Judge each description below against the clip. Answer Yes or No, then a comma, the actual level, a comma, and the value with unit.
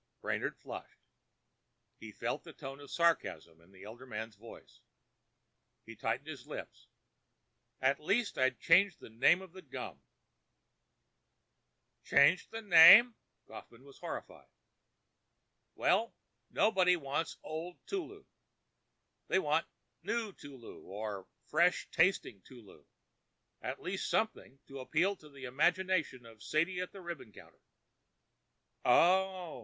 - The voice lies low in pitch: No, medium, 160 Hz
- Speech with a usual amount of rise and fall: No, wide, 6.8 semitones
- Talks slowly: Yes, slow, 120 wpm